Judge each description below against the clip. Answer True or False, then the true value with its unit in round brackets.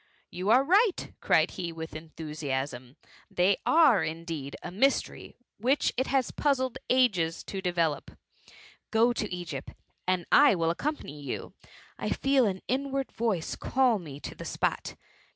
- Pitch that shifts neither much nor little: False (8.1 semitones)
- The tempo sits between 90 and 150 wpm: True (145 wpm)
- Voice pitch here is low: False (190 Hz)